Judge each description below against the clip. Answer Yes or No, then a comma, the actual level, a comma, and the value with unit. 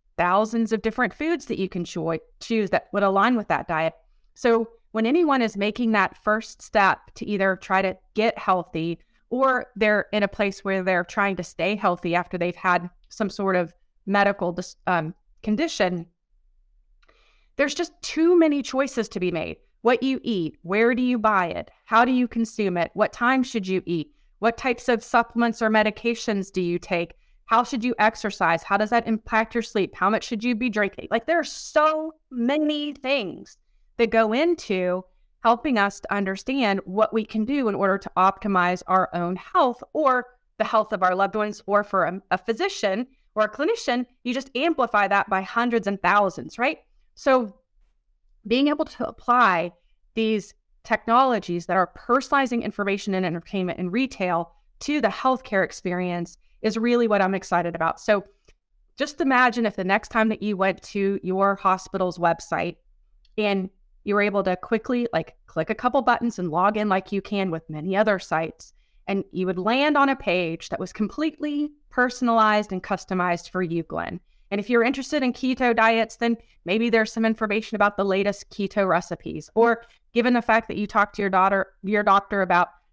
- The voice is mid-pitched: No, high, 210 Hz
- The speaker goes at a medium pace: Yes, average, 185 wpm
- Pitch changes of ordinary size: Yes, average, 4.2 semitones